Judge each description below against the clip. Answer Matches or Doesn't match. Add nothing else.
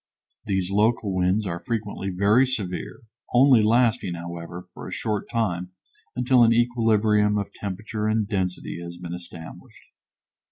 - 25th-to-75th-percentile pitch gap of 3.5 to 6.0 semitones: Matches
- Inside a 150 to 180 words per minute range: Doesn't match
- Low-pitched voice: Matches